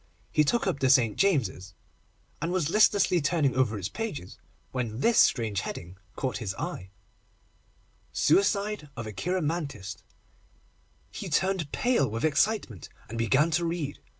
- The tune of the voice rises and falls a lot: Yes, wide, 8.3 semitones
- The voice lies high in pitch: No, medium, 140 Hz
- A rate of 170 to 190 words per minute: No, average, 140 wpm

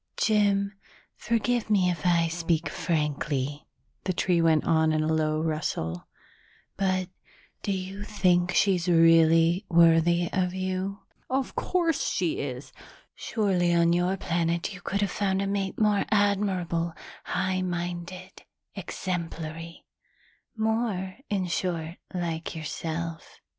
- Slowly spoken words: Yes, slow, 120 wpm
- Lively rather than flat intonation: No, average, 2.8 semitones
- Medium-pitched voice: Yes, medium, 175 Hz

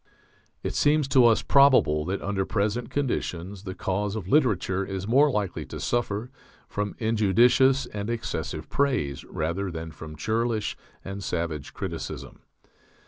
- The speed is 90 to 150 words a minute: Yes, average, 140 wpm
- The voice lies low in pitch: Yes, low, 105 Hz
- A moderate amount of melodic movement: Yes, average, 4.6 semitones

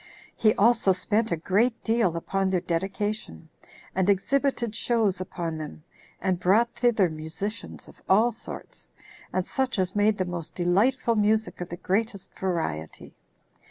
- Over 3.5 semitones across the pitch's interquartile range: Yes, average, 4.1 semitones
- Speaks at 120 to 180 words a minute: Yes, average, 145 wpm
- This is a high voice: Yes, high, 195 Hz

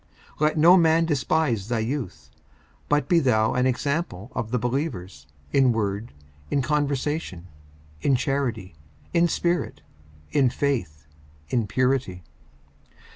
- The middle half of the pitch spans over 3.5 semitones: Yes, average, 5.1 semitones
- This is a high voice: No, low, 130 Hz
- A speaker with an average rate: No, slow, 125 wpm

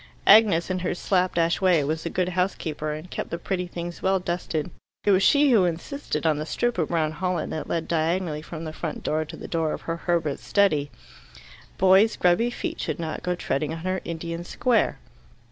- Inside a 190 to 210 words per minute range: Yes, average, 200 wpm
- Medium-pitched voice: Yes, medium, 175 Hz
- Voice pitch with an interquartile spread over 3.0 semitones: No, average, 2.7 semitones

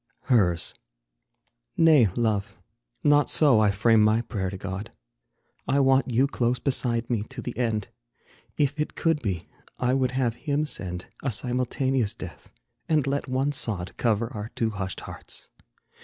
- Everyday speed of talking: Yes, average, 155 wpm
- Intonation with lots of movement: No, average, 4.2 semitones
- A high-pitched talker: No, low, 120 Hz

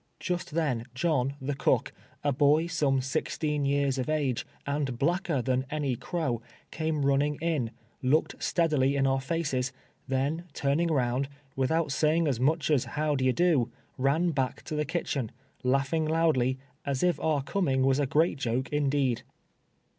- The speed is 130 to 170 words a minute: Yes, average, 160 wpm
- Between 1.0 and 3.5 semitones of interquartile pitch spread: Yes, average, 3.0 semitones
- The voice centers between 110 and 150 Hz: Yes, medium, 140 Hz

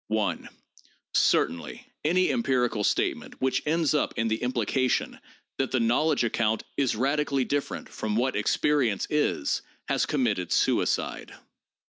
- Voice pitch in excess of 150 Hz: No, low, 130 Hz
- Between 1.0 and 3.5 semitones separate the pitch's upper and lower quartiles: No, average, 4.6 semitones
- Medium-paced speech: No, slow, 125 wpm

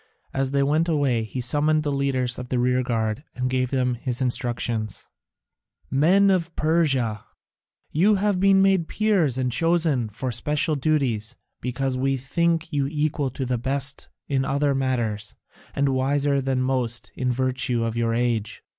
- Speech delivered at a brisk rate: No, average, 155 wpm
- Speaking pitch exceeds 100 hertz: Yes, low, 135 Hz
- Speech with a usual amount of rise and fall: Yes, average, 3.4 semitones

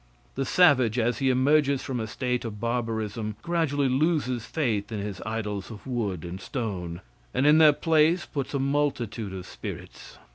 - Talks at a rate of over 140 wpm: Yes, average, 170 wpm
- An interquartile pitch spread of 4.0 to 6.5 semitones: Yes, average, 5.1 semitones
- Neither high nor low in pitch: No, low, 125 Hz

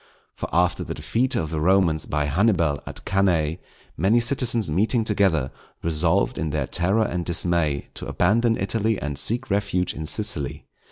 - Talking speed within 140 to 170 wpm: Yes, average, 160 wpm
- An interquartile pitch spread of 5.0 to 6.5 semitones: Yes, wide, 5.5 semitones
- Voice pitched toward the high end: No, very low, 90 Hz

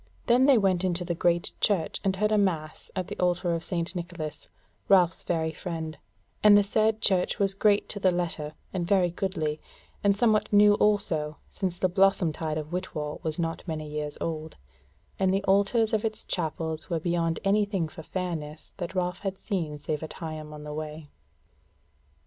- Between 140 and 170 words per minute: No, average, 185 wpm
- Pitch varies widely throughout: No, average, 3.7 semitones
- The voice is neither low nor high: Yes, medium, 175 Hz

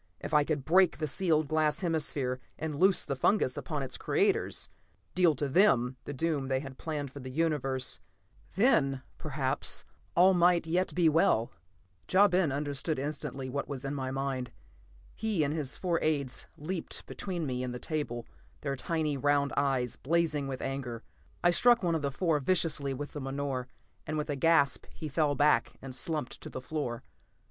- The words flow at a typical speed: Yes, average, 180 wpm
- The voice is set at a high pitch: No, medium, 145 Hz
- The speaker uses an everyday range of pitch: Yes, average, 3.5 semitones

